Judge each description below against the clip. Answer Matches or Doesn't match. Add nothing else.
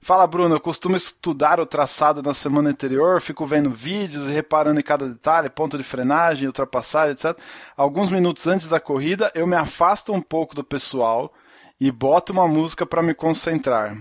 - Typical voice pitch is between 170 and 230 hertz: Doesn't match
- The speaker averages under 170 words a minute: Doesn't match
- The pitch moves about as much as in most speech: Matches